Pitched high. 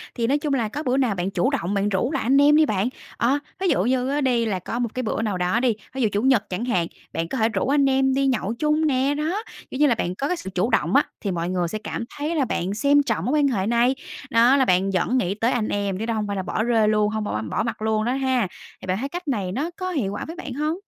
Yes: high, 235 Hz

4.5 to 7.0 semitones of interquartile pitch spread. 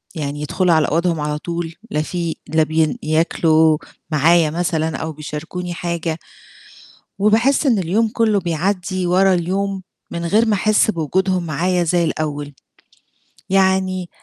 No: average, 3.0 semitones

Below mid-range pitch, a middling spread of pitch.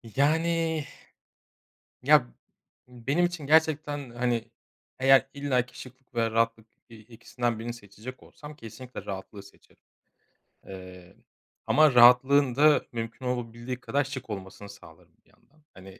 Yes: low, 125 Hz; average, 4.0 semitones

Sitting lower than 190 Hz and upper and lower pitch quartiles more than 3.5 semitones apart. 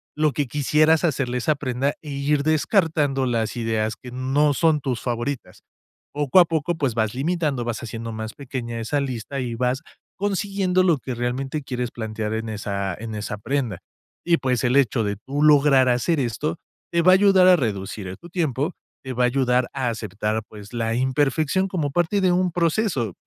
Yes: low, 135 Hz; average, 4.9 semitones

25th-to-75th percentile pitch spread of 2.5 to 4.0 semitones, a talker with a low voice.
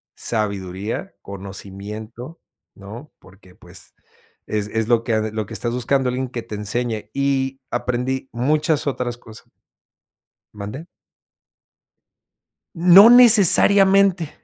No: average, 4.8 semitones; low, 120 Hz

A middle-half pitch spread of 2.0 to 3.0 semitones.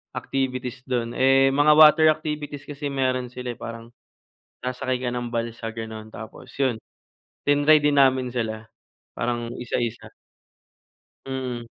Yes: average, 2.7 semitones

